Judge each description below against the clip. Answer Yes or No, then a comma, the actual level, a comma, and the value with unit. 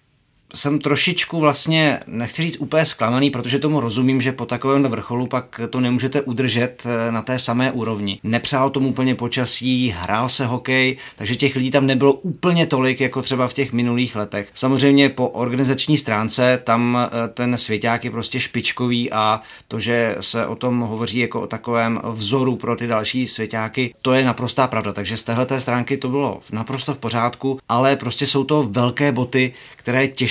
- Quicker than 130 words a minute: Yes, fast, 170 wpm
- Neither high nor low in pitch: No, low, 125 Hz